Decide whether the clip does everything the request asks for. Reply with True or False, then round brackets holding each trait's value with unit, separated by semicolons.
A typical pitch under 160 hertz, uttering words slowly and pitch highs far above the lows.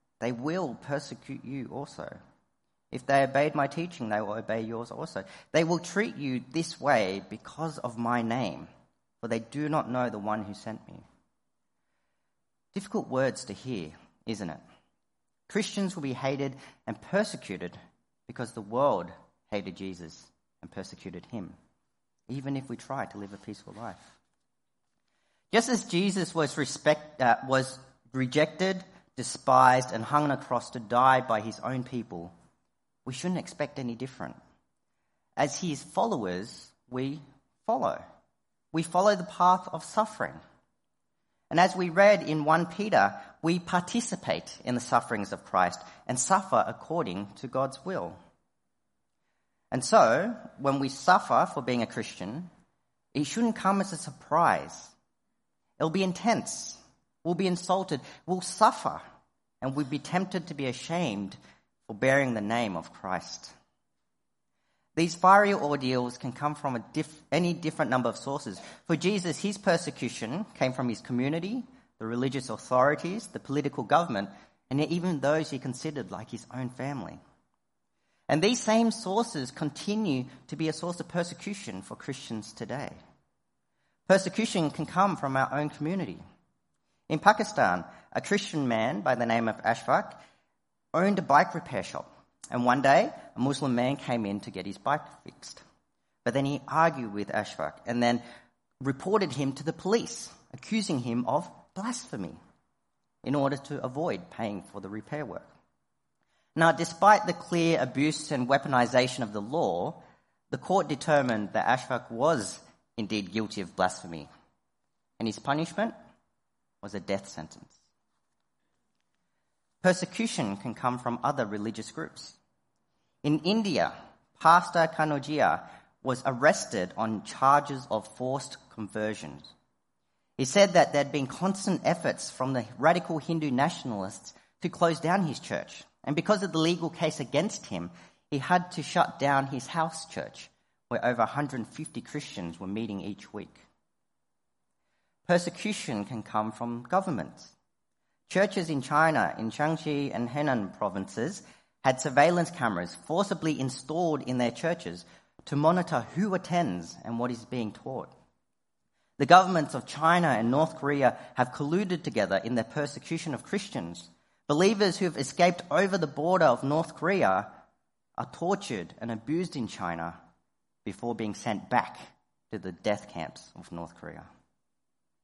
False (140 Hz; 145 wpm; 6.7 semitones)